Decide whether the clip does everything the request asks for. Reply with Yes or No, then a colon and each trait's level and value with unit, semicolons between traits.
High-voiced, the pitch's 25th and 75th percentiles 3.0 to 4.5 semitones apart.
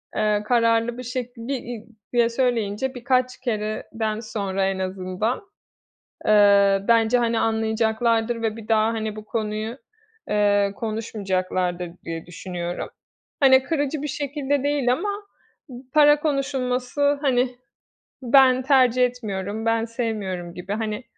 Yes: high, 230 Hz; average, 3.3 semitones